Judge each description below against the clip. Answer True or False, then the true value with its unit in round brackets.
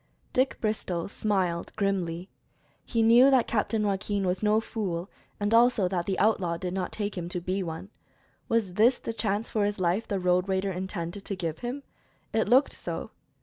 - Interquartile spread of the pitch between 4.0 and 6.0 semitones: False (3.5 semitones)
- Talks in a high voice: True (200 Hz)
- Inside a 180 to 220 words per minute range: True (185 wpm)